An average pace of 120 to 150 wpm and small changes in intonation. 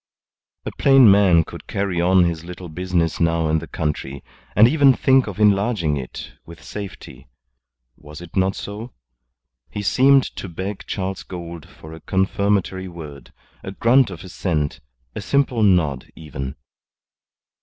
No: average, 145 wpm; average, 4.2 semitones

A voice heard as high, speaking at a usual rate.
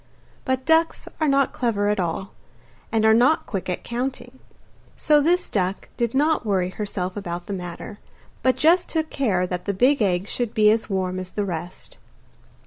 Yes: high, 215 Hz; average, 180 wpm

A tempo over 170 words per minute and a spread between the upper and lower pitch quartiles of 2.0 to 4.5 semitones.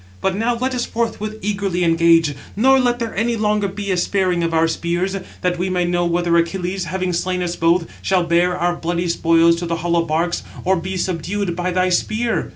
Yes: fast, 205 wpm; average, 2.8 semitones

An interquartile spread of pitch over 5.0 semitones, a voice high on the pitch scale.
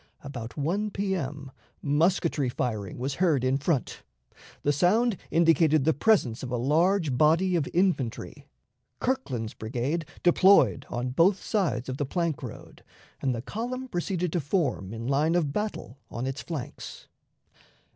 No: wide, 5.6 semitones; medium, 150 Hz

